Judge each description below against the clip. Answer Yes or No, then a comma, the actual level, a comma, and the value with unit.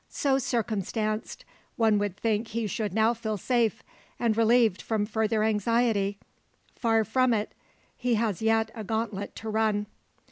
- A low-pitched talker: No, high, 220 Hz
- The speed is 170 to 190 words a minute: No, average, 145 wpm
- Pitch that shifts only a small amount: Yes, narrow, 1.5 semitones